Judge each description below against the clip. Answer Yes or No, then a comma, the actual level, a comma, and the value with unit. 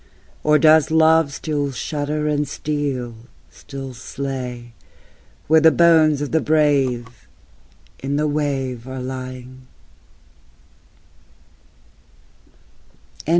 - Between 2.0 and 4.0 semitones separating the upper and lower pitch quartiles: Yes, average, 2.9 semitones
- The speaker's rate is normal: No, slow, 90 wpm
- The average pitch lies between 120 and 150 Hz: Yes, medium, 140 Hz